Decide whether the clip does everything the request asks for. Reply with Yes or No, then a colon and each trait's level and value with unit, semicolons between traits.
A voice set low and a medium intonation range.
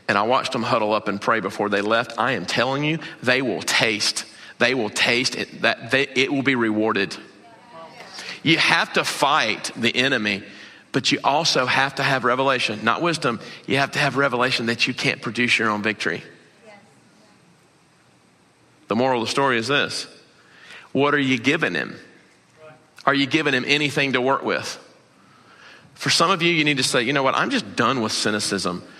Yes: low, 130 Hz; average, 3.5 semitones